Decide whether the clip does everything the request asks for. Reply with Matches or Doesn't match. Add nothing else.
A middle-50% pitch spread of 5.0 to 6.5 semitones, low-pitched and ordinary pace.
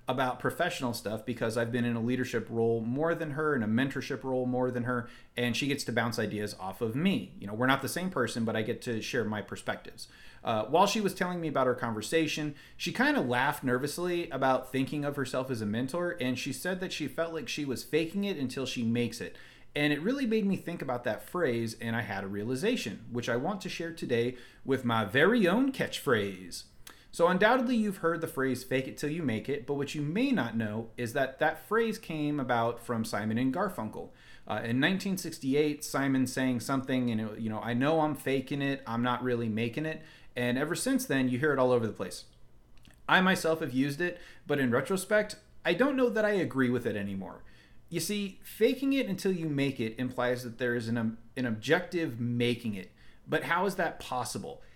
Doesn't match